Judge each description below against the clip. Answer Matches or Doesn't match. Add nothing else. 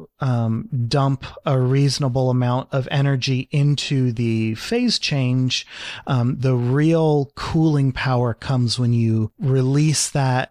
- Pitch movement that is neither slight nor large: Doesn't match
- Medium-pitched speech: Doesn't match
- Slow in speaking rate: Matches